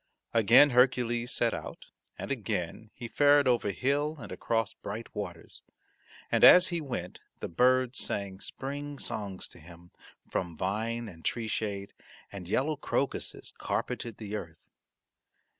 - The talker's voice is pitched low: Yes, low, 115 Hz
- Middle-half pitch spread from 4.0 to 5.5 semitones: Yes, average, 4.7 semitones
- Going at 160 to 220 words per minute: No, average, 140 wpm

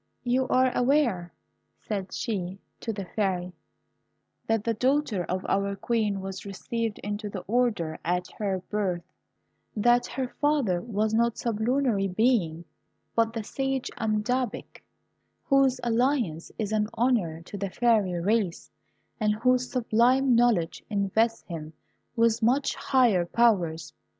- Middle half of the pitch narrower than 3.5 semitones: No, average, 4.1 semitones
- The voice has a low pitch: No, high, 220 Hz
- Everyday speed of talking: No, slow, 130 wpm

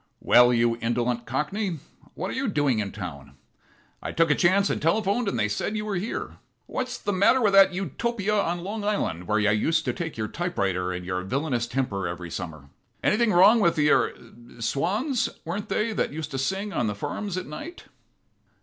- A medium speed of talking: Yes, average, 195 wpm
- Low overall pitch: No, medium, 160 Hz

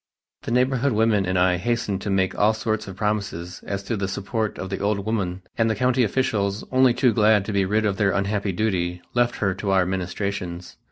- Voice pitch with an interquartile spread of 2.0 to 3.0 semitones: Yes, average, 2.7 semitones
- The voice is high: No, low, 100 Hz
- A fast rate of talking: Yes, fast, 215 wpm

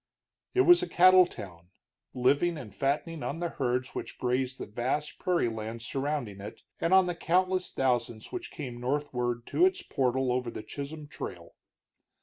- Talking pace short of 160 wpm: No, average, 165 wpm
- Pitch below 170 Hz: Yes, low, 135 Hz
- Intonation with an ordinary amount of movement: No, wide, 5.9 semitones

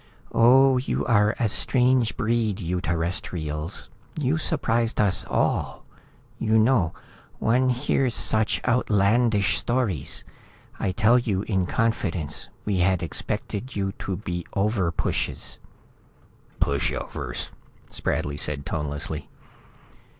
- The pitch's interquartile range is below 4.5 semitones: No, average, 5.2 semitones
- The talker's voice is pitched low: Yes, low, 105 Hz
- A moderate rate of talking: No, slow, 105 wpm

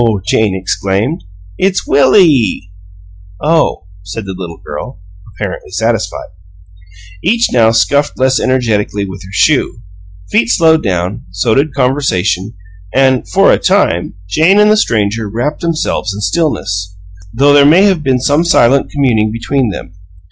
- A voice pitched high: No, low, 115 Hz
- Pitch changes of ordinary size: No, wide, 6.5 semitones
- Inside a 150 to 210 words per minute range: No, average, 140 wpm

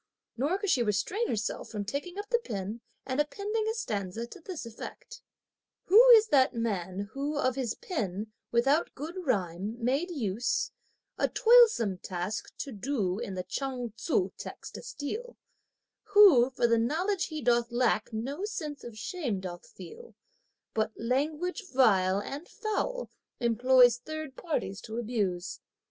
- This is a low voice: No, very high, 250 Hz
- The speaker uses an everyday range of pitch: No, wide, 7.6 semitones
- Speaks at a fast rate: No, average, 150 wpm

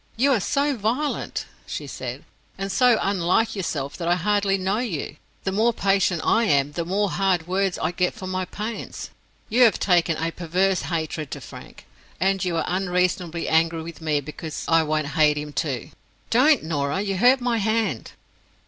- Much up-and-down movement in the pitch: No, average, 4.3 semitones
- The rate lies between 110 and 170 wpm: No, average, 180 wpm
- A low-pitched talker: No, medium, 185 Hz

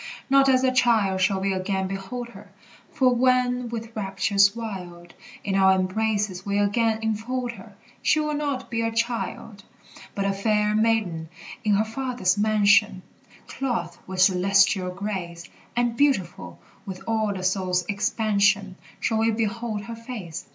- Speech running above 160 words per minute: No, average, 150 wpm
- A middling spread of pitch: Yes, average, 3.3 semitones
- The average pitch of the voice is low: No, high, 210 Hz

